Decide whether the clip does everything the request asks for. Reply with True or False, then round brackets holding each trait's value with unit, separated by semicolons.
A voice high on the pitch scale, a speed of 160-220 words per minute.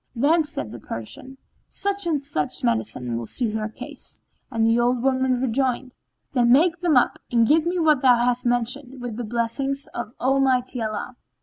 True (250 Hz; 180 wpm)